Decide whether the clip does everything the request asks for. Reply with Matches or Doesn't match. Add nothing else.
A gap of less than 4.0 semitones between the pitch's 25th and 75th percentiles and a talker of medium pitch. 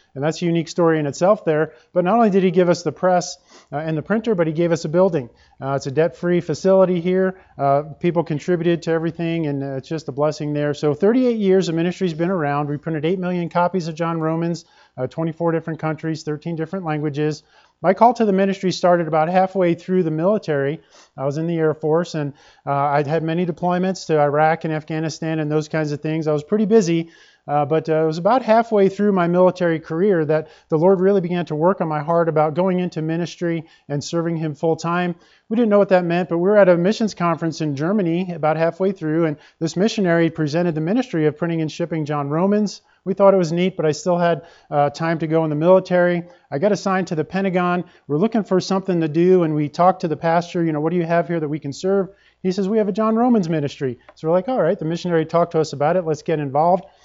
Matches